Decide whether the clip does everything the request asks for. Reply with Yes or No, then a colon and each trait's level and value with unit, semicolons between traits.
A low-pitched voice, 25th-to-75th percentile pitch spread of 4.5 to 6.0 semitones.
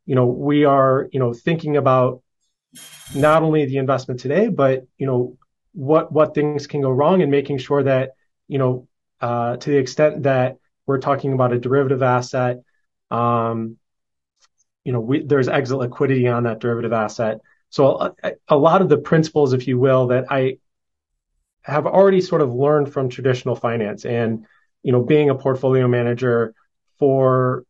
No: low, 130 Hz; narrow, 2.6 semitones